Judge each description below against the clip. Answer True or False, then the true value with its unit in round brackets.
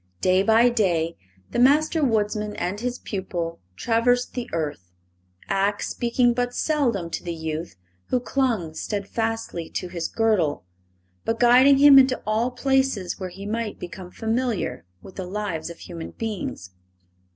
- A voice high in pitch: True (215 Hz)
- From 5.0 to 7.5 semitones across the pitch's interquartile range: True (5.6 semitones)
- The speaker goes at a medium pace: True (145 wpm)